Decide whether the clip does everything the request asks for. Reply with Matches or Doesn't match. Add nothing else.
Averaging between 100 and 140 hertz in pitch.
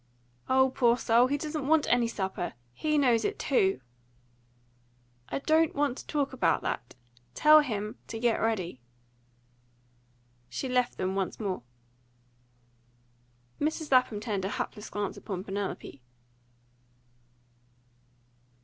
Doesn't match